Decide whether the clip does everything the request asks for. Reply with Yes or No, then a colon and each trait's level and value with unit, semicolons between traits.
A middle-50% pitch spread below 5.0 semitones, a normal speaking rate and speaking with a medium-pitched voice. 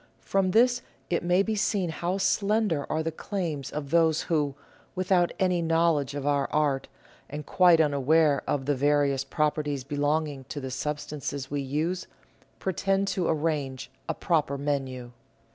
Yes: average, 3.7 semitones; average, 150 wpm; medium, 150 Hz